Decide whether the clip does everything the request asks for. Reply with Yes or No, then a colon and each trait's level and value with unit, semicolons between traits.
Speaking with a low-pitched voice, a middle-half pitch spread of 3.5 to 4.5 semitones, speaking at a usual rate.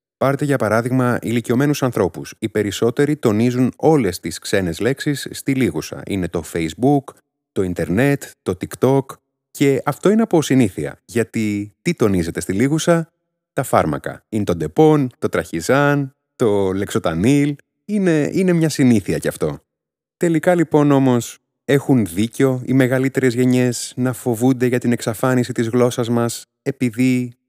Yes: low, 125 Hz; average, 3.8 semitones; average, 140 wpm